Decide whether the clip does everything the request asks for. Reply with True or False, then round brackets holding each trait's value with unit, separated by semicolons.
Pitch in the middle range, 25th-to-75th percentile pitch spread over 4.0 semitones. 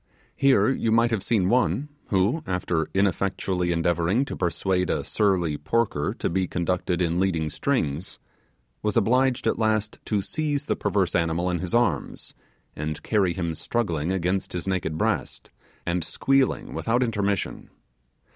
False (95 Hz; 4.7 semitones)